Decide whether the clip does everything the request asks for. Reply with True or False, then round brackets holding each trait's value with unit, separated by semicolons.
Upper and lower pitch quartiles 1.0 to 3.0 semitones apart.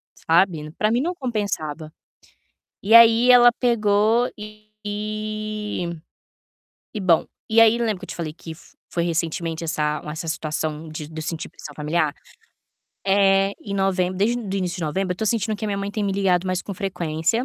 False (4.4 semitones)